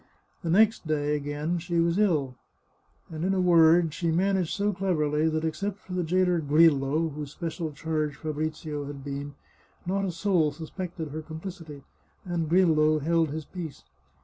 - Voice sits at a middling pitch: Yes, medium, 160 Hz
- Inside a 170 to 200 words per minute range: No, average, 160 wpm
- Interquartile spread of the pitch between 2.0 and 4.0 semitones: Yes, average, 2.8 semitones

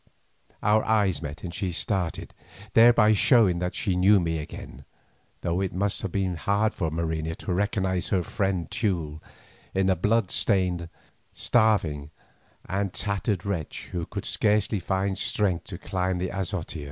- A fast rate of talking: No, average, 150 wpm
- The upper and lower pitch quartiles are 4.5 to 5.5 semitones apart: No, average, 3.0 semitones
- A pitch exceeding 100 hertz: No, very low, 95 Hz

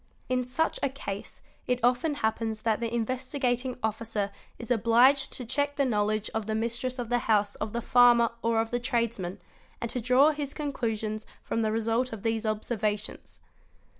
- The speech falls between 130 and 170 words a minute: No, average, 180 wpm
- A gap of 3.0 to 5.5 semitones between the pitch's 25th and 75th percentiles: No, narrow, 2.4 semitones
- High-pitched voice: Yes, high, 235 Hz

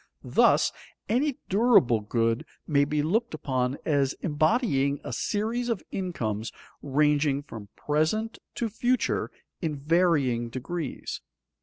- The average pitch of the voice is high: No, medium, 150 Hz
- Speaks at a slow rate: Yes, slow, 115 wpm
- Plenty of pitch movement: Yes, wide, 7.4 semitones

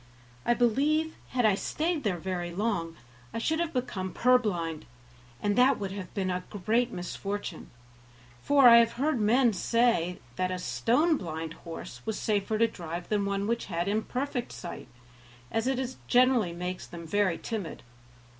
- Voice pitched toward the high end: Yes, high, 210 Hz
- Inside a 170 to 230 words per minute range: No, average, 160 wpm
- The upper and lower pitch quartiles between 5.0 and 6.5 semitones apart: Yes, wide, 5.4 semitones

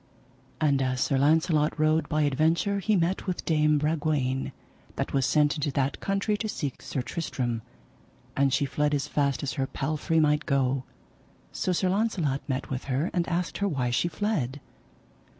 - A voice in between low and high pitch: Yes, medium, 150 Hz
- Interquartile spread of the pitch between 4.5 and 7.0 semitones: No, average, 3.7 semitones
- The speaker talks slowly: No, average, 170 wpm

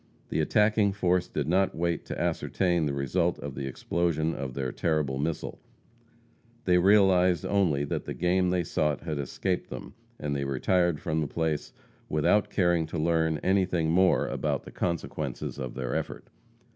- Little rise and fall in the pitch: No, average, 3.6 semitones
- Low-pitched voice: Yes, very low, 85 Hz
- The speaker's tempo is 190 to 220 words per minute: No, average, 165 wpm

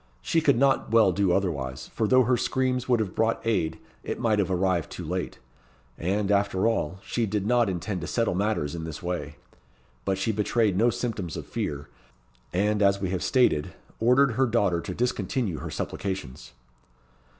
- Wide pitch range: No, average, 4.3 semitones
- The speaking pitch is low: Yes, low, 100 Hz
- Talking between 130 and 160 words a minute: No, average, 180 wpm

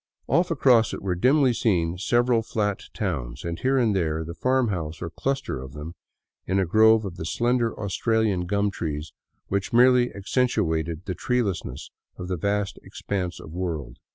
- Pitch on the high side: No, low, 100 Hz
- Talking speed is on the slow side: No, average, 180 wpm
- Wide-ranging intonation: Yes, wide, 5.9 semitones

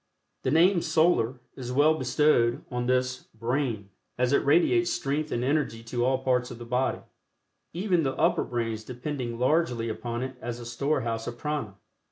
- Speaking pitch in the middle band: No, low, 125 Hz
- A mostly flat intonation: No, average, 4.1 semitones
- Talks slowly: No, average, 170 wpm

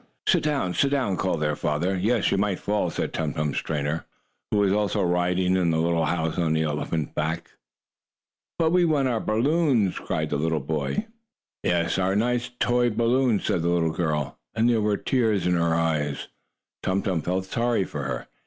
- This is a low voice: Yes, very low, 95 Hz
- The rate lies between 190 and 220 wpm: Yes, average, 195 wpm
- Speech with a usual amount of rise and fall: No, wide, 6.0 semitones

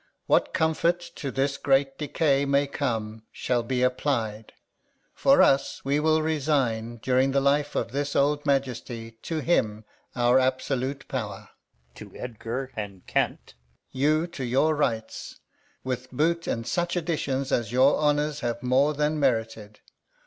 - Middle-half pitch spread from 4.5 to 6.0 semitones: No, average, 3.5 semitones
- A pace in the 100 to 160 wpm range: Yes, average, 140 wpm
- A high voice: No, low, 135 Hz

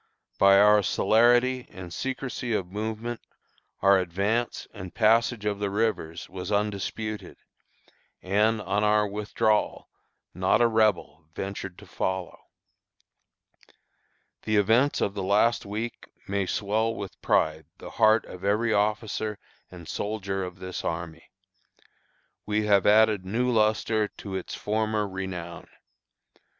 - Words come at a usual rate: No, slow, 125 wpm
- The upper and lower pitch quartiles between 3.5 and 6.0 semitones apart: No, narrow, 2.5 semitones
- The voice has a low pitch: Yes, low, 105 Hz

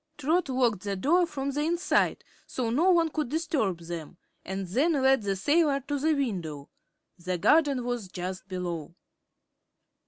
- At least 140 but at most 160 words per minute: Yes, average, 155 wpm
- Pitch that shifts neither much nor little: No, wide, 8.4 semitones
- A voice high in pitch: Yes, very high, 255 Hz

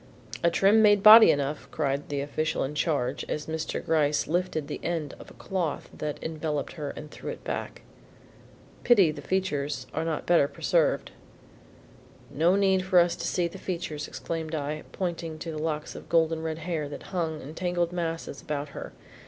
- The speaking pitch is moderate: Yes, medium, 160 Hz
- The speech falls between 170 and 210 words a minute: Yes, average, 180 wpm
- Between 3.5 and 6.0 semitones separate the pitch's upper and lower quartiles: No, average, 2.7 semitones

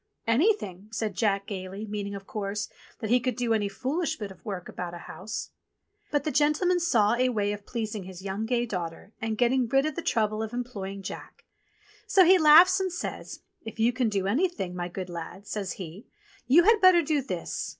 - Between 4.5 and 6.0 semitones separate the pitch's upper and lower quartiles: Yes, wide, 5.5 semitones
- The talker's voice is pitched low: No, high, 220 Hz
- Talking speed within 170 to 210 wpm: Yes, average, 200 wpm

